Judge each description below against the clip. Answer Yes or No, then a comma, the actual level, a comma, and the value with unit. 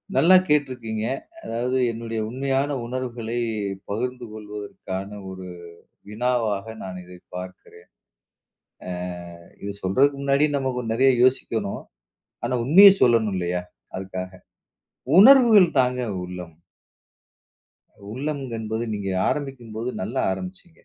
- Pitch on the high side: No, low, 115 Hz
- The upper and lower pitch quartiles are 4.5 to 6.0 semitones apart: Yes, average, 5.2 semitones